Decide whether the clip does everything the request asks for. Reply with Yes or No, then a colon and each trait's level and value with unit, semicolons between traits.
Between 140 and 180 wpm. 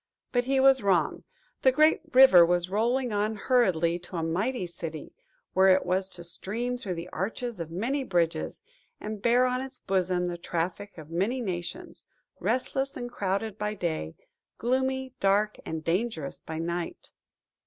Yes: average, 160 wpm